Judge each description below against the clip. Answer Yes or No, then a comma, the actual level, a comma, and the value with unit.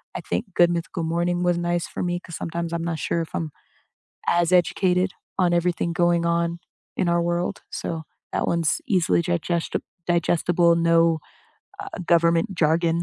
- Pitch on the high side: No, medium, 170 Hz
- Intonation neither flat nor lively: No, narrow, 0.7 semitones